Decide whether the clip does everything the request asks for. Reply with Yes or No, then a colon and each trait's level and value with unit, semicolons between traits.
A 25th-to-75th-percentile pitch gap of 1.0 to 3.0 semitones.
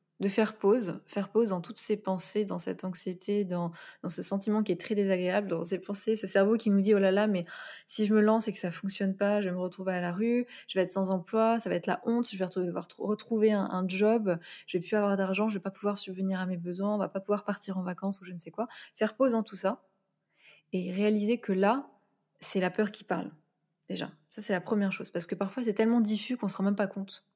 Yes: narrow, 2.4 semitones